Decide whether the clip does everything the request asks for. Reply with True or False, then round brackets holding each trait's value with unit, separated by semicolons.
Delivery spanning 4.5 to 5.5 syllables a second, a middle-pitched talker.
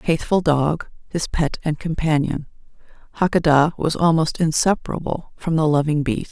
True (4.9 syllables/s; 160 Hz)